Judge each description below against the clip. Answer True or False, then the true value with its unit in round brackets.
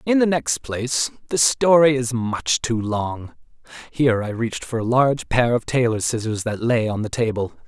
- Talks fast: False (195 wpm)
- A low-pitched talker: True (120 Hz)